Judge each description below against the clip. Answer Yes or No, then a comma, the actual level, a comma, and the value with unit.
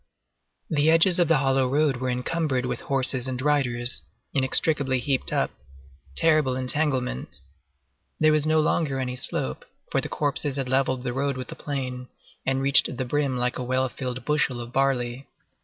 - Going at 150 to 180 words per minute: Yes, average, 170 wpm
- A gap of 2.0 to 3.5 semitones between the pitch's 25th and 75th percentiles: Yes, narrow, 2.5 semitones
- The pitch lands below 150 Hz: Yes, low, 135 Hz